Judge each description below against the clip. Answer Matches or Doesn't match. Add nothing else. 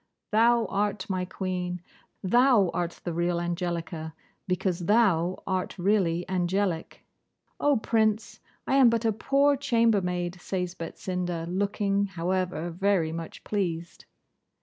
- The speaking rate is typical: Doesn't match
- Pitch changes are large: Doesn't match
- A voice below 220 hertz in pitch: Matches